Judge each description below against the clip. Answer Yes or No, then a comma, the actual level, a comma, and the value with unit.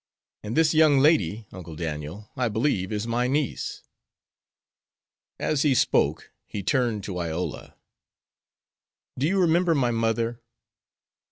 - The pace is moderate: No, slow, 120 wpm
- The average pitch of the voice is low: Yes, low, 115 Hz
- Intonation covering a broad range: Yes, wide, 6.5 semitones